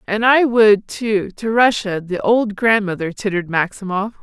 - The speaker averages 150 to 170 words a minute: Yes, average, 155 wpm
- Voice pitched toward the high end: Yes, high, 210 Hz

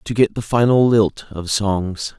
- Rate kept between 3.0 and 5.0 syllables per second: Yes, 4.0 syllables/s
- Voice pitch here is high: No, low, 105 Hz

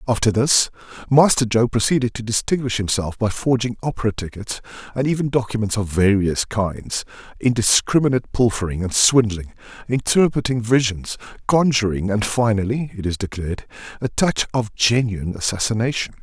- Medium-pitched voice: No, low, 115 Hz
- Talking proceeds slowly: Yes, slow, 130 wpm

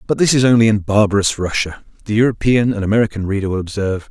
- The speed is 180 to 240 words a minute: Yes, fast, 205 wpm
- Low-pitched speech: Yes, low, 105 Hz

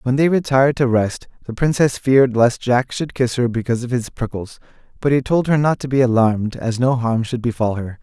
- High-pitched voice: No, low, 125 Hz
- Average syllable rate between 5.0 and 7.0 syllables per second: Yes, 5.6 syllables/s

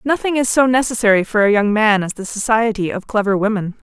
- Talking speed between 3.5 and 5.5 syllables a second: No, 6.0 syllables/s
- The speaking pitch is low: No, high, 220 Hz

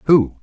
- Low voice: Yes, low, 130 Hz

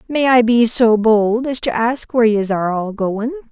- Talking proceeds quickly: Yes, fast, 220 wpm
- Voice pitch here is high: Yes, high, 230 Hz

